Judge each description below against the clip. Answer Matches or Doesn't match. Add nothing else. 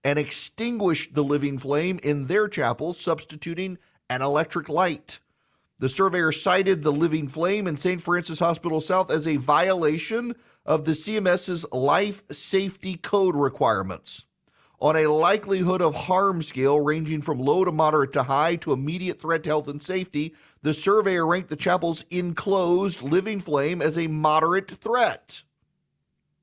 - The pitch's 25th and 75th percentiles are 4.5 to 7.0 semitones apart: Doesn't match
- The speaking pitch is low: Doesn't match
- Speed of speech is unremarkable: Matches